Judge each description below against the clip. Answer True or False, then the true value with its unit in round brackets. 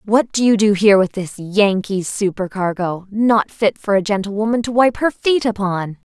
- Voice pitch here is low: False (205 Hz)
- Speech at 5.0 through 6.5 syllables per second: False (4.8 syllables/s)